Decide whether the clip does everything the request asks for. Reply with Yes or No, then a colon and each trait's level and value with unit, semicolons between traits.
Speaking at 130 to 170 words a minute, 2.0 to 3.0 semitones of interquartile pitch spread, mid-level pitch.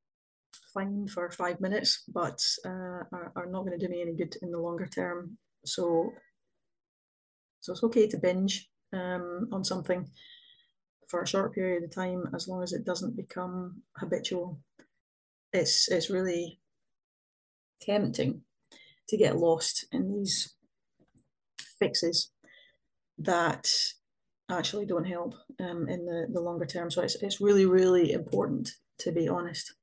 Yes: average, 140 wpm; narrow, 2.4 semitones; medium, 180 Hz